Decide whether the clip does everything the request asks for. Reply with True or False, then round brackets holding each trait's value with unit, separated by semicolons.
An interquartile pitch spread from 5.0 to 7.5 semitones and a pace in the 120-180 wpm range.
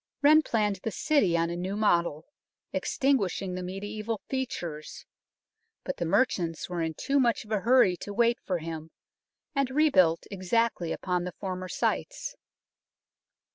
True (5.3 semitones; 145 wpm)